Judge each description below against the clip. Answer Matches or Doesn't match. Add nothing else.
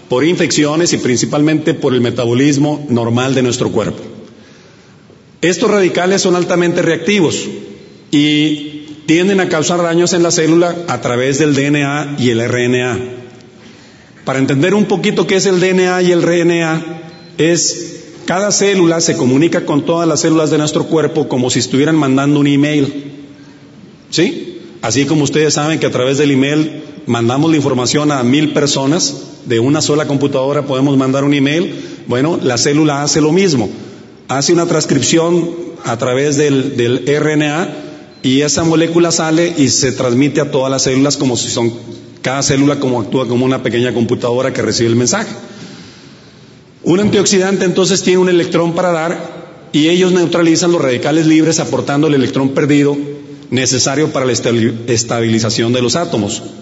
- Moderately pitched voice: Matches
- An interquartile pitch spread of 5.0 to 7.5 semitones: Doesn't match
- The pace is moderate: Matches